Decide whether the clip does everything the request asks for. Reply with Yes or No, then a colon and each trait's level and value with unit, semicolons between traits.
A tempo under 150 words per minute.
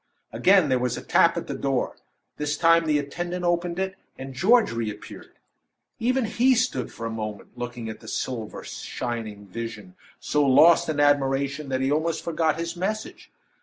No: average, 175 wpm